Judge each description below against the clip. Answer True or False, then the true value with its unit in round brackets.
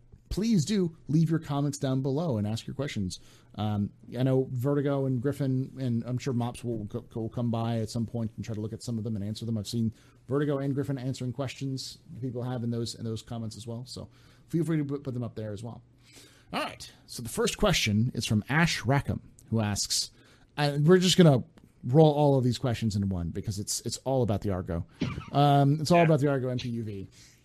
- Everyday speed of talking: False (225 wpm)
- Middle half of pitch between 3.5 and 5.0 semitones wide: True (3.8 semitones)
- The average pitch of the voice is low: True (125 Hz)